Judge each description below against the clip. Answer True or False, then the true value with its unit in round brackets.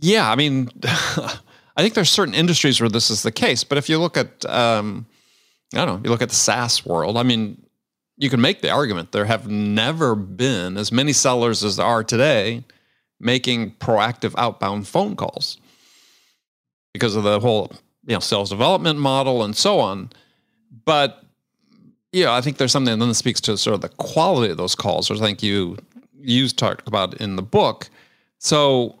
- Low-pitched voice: True (120 Hz)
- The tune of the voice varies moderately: True (3.8 semitones)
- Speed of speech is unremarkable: True (190 wpm)